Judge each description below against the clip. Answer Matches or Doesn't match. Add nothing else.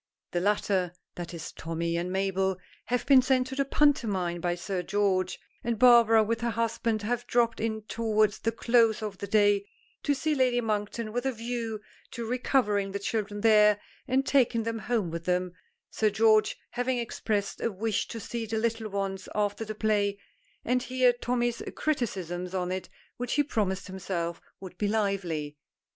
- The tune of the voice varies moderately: Matches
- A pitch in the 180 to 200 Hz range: Doesn't match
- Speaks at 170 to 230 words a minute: Matches